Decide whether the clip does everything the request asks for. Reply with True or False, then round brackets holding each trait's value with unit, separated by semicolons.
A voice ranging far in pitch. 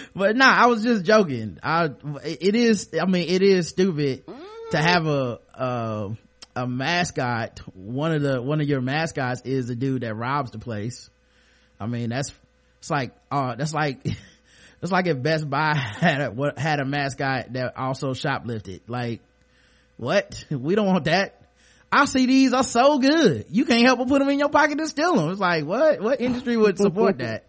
True (8.6 semitones)